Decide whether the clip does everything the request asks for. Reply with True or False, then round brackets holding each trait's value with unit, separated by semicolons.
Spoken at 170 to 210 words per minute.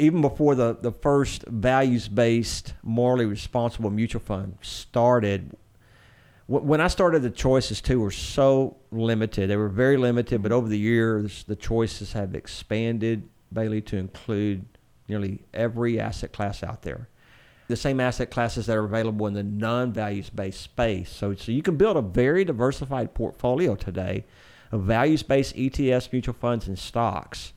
False (160 wpm)